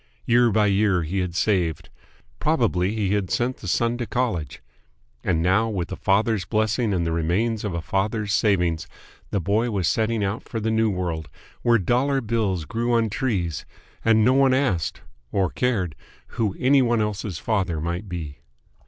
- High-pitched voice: No, low, 105 Hz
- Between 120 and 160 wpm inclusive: No, average, 175 wpm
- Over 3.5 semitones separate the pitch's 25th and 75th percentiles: Yes, average, 4.5 semitones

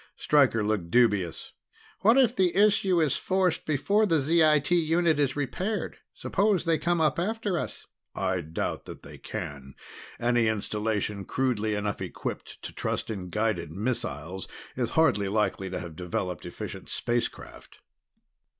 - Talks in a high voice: No, low, 125 Hz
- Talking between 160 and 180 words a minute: No, average, 145 wpm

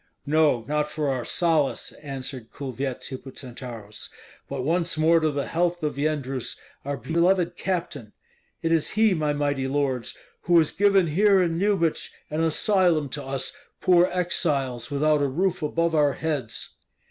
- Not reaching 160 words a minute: Yes, average, 150 wpm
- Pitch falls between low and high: Yes, medium, 150 Hz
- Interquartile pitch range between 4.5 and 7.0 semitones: No, average, 3.8 semitones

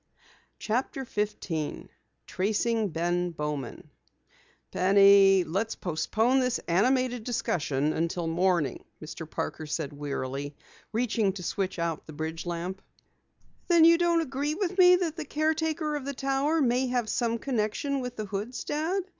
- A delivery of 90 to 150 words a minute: Yes, average, 140 wpm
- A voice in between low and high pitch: No, high, 215 Hz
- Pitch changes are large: Yes, wide, 8.1 semitones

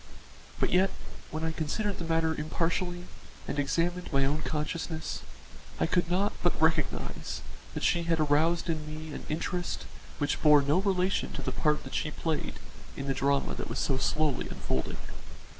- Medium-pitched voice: Yes, medium, 160 Hz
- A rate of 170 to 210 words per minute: Yes, average, 175 wpm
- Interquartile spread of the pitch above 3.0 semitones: No, average, 2.7 semitones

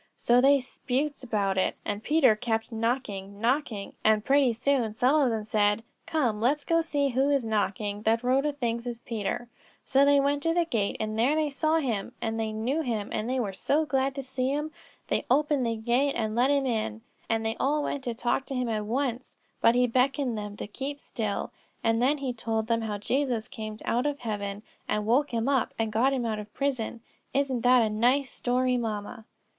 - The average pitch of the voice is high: Yes, high, 245 Hz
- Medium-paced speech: No, fast, 215 wpm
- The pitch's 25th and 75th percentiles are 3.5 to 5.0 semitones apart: Yes, average, 3.9 semitones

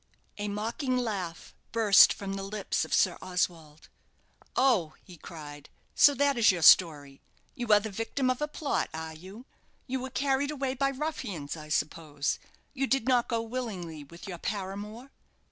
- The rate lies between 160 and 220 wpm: Yes, average, 165 wpm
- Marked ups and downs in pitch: Yes, wide, 7.2 semitones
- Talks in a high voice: Yes, high, 210 Hz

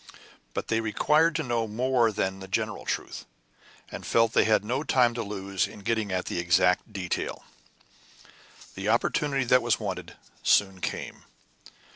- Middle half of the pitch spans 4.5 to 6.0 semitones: No, average, 3.8 semitones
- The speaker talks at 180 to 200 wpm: No, average, 160 wpm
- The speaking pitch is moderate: No, low, 110 Hz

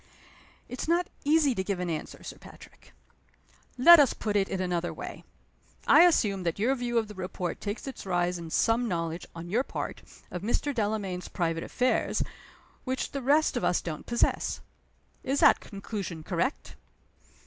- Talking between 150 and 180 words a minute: Yes, average, 170 wpm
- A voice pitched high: Yes, high, 205 Hz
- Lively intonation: Yes, wide, 6.3 semitones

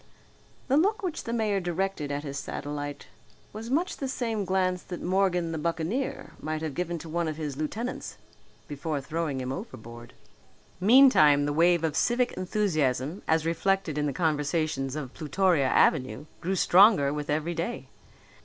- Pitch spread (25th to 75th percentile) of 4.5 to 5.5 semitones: Yes, average, 4.8 semitones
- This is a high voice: No, medium, 165 Hz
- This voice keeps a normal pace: Yes, average, 160 wpm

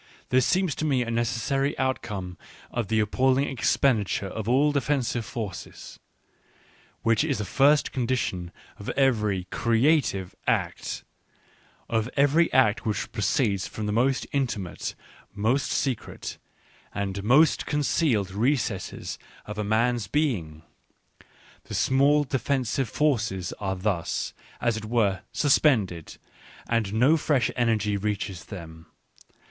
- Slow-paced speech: Yes, slow, 120 wpm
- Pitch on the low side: Yes, low, 115 Hz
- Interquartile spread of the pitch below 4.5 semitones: No, average, 5.0 semitones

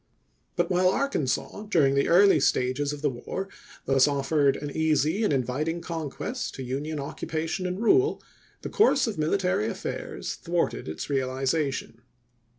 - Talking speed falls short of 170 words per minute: Yes, average, 150 wpm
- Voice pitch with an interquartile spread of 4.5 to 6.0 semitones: Yes, average, 5.1 semitones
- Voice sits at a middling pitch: Yes, medium, 150 Hz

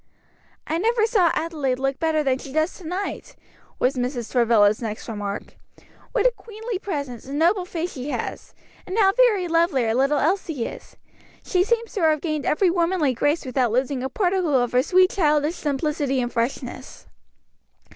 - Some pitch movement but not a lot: No, wide, 5.9 semitones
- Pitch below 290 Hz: No, very high, 305 Hz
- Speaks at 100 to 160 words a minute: No, average, 175 wpm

